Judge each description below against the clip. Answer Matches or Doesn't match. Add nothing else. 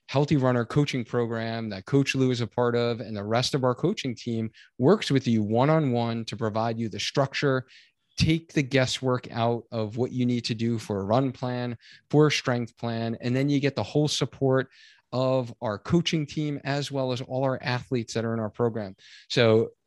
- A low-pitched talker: Matches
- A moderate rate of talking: Doesn't match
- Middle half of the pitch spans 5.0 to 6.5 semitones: Doesn't match